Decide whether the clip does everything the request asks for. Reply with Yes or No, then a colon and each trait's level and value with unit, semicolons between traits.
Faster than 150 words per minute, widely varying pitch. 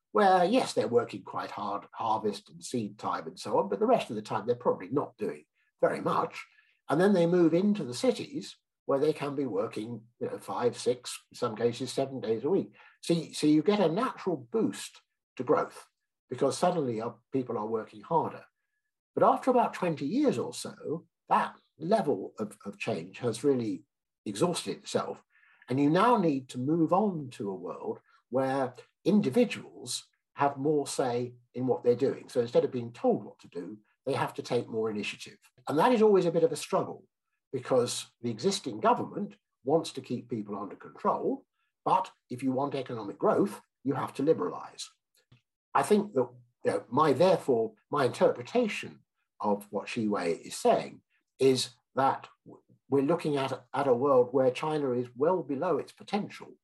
Yes: average, 180 wpm; wide, 8.8 semitones